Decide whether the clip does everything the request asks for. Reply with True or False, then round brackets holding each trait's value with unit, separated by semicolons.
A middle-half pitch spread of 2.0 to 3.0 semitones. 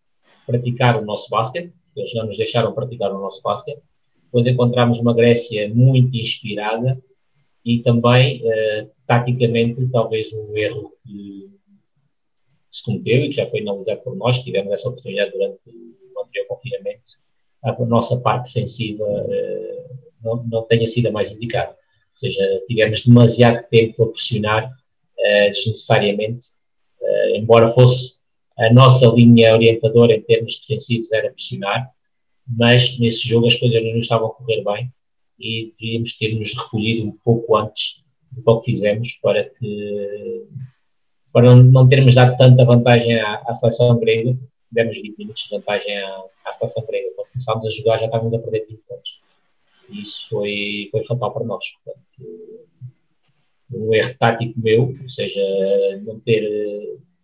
True (2.6 semitones)